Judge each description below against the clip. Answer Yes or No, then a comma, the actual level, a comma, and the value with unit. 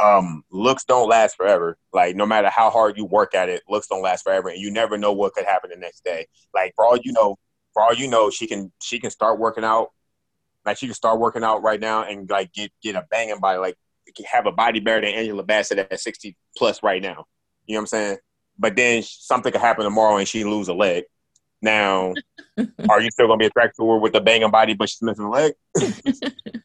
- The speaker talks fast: Yes, fast, 240 wpm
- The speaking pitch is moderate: No, low, 110 Hz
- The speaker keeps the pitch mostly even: Yes, narrow, 2.2 semitones